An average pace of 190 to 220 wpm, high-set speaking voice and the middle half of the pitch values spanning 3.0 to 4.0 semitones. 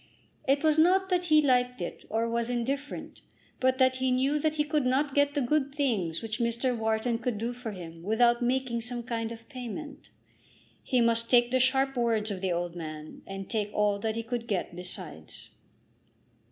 Yes: average, 195 wpm; high, 240 Hz; average, 3.4 semitones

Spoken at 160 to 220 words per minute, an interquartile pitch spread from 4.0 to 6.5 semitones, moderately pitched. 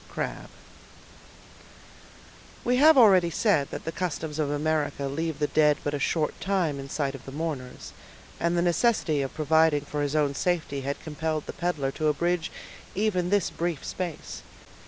No: average, 165 wpm; average, 3.3 semitones; medium, 155 Hz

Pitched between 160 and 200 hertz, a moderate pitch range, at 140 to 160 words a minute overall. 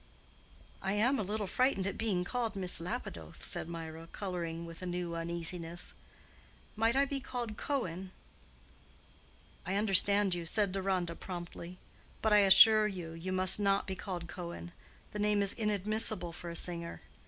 Yes: high, 190 Hz; average, 3.5 semitones; average, 155 wpm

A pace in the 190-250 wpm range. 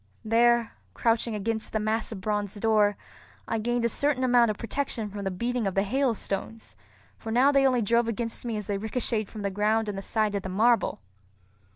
Yes: average, 200 wpm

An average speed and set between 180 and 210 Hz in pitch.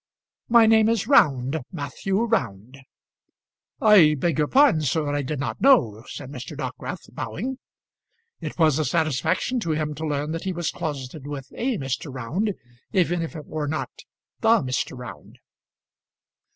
No: average, 155 wpm; medium, 155 Hz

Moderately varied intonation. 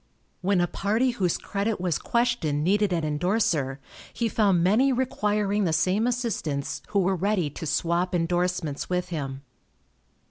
Yes: average, 4.2 semitones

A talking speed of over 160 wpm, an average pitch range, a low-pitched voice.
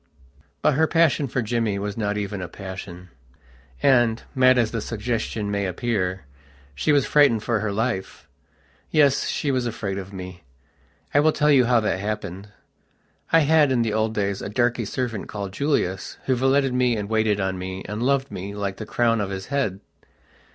Yes: average, 185 wpm; average, 4.4 semitones; low, 110 Hz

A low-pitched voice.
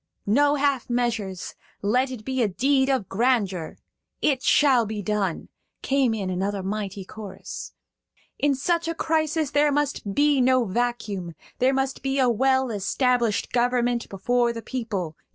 No: high, 245 Hz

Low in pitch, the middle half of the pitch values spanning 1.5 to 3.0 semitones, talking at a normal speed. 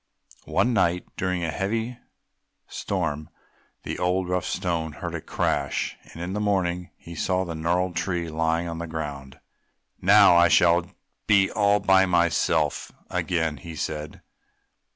Yes: very low, 85 Hz; narrow, 2.5 semitones; average, 145 wpm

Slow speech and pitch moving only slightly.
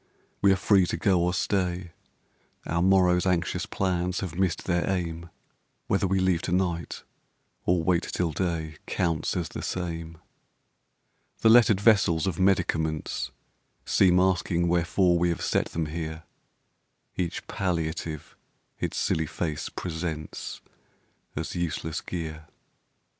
Yes: slow, 130 wpm; narrow, 2.1 semitones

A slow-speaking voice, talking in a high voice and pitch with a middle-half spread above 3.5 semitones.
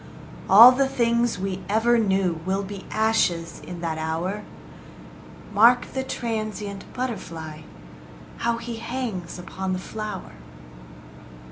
Yes: slow, 115 wpm; high, 205 Hz; average, 4.2 semitones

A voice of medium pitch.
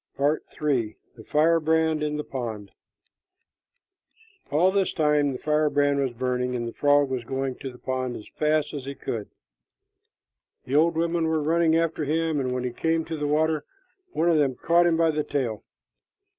Yes: medium, 150 Hz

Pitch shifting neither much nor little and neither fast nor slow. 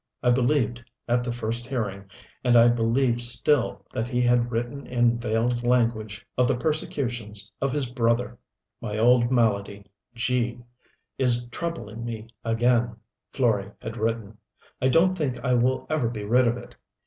No: narrow, 1.7 semitones; average, 155 wpm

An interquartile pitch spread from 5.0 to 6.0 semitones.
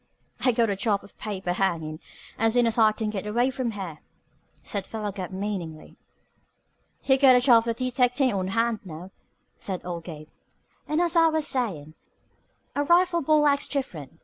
Yes: wide, 5.6 semitones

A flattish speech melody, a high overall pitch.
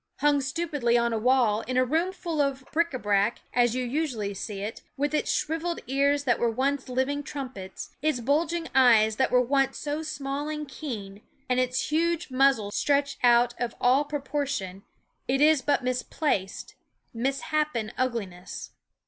No: average, 3.7 semitones; very high, 265 Hz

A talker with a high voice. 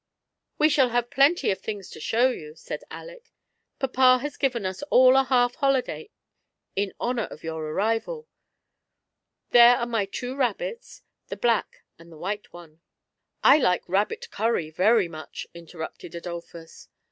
Yes: high, 235 Hz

